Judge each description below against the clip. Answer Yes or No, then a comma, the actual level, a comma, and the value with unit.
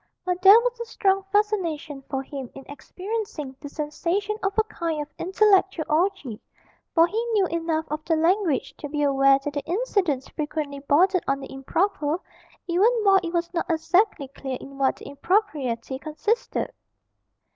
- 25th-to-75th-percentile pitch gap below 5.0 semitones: No, wide, 5.4 semitones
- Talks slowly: No, average, 165 wpm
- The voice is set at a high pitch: Yes, very high, 330 Hz